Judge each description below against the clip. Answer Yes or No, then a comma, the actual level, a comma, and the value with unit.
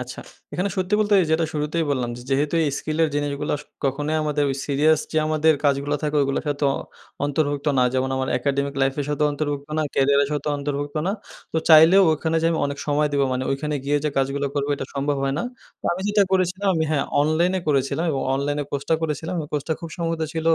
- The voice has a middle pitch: Yes, medium, 150 Hz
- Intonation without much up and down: Yes, narrow, 2.2 semitones